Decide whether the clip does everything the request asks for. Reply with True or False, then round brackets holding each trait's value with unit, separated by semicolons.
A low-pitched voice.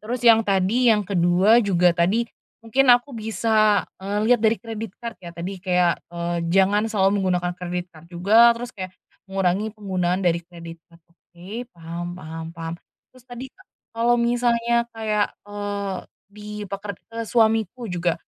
False (200 Hz)